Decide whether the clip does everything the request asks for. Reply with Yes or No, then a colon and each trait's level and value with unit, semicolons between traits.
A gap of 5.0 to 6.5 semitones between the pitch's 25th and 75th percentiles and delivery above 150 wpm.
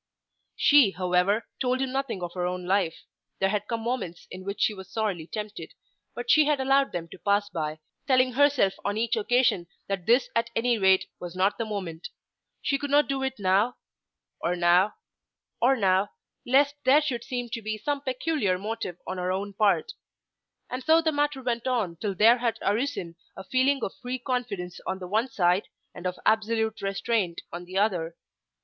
Yes: wide, 5.5 semitones; average, 190 wpm